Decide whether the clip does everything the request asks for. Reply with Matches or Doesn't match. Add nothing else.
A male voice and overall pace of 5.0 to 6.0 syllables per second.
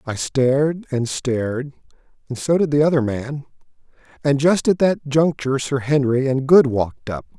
Doesn't match